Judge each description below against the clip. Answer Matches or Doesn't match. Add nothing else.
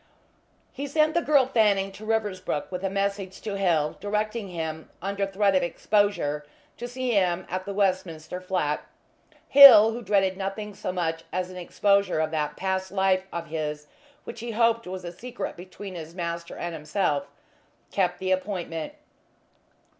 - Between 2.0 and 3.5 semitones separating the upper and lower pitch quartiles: Matches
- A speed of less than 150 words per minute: Doesn't match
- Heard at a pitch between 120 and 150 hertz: Doesn't match